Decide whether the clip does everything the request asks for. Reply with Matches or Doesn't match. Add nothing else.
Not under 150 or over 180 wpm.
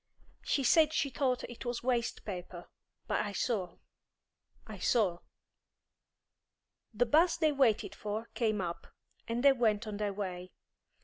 Doesn't match